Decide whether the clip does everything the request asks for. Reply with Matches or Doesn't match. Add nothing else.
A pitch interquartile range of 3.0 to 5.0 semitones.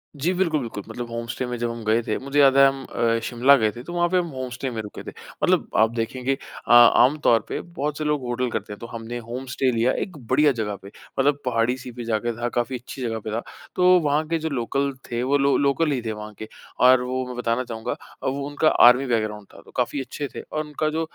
Matches